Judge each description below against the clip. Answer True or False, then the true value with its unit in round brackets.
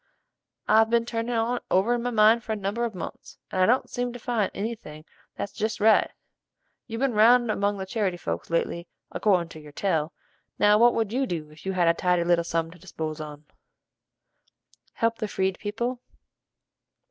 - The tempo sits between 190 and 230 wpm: True (195 wpm)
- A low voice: False (205 Hz)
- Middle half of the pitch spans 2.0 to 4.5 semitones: False (5.0 semitones)